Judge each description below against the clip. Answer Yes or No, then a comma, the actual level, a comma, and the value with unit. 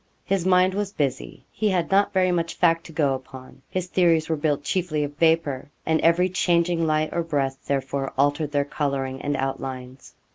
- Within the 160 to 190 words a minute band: Yes, average, 185 wpm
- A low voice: No, medium, 155 Hz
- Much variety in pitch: No, average, 4.0 semitones